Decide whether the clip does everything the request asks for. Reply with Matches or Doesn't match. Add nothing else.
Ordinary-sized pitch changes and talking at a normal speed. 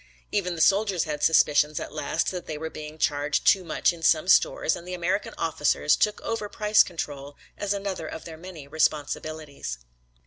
Matches